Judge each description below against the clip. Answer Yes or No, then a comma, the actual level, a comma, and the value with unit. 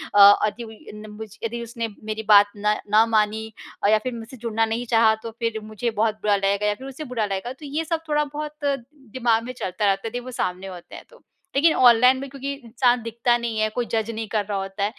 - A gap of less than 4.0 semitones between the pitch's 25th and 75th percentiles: Yes, average, 2.9 semitones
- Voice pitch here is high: Yes, high, 225 Hz